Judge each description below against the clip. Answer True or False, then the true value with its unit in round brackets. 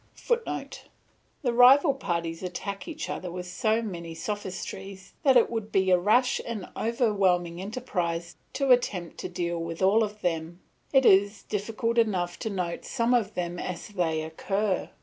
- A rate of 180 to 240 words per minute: False (160 wpm)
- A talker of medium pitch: False (195 Hz)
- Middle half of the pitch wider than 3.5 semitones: True (4.7 semitones)